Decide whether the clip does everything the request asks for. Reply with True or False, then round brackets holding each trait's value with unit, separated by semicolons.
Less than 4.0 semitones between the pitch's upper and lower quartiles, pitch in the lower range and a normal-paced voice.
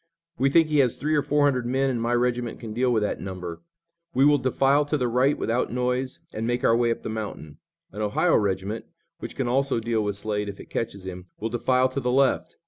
False (3.6 semitones; 120 Hz; 235 wpm)